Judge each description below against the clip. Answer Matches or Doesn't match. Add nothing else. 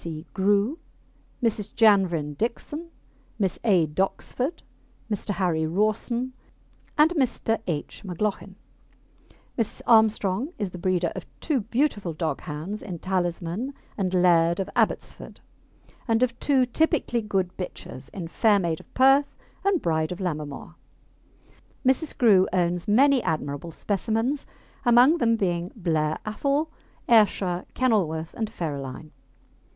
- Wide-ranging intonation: Matches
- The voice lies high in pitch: Matches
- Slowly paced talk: Matches